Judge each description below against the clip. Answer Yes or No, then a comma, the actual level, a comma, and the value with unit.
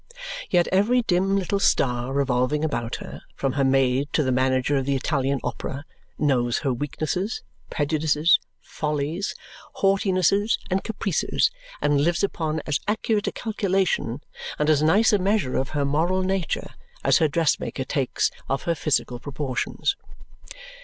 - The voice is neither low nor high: Yes, medium, 150 Hz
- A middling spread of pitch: No, wide, 5.7 semitones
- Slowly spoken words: No, average, 145 wpm